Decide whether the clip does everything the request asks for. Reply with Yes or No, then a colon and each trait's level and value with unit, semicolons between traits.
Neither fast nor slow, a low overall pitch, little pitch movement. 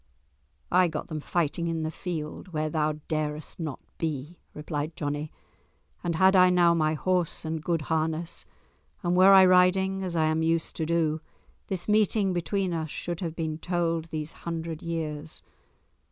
No: average, 165 wpm; medium, 165 Hz; narrow, 2.3 semitones